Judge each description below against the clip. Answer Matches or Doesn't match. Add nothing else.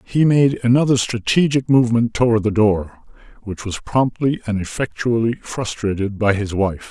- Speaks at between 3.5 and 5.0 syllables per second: Matches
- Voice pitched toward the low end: Matches